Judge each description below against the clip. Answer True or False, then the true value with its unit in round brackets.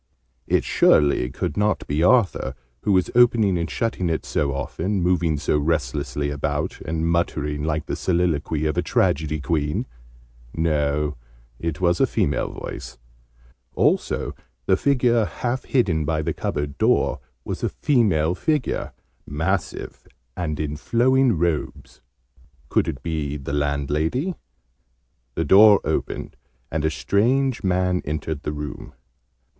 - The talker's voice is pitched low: True (80 Hz)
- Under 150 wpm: True (135 wpm)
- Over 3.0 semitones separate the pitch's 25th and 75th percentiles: True (4.9 semitones)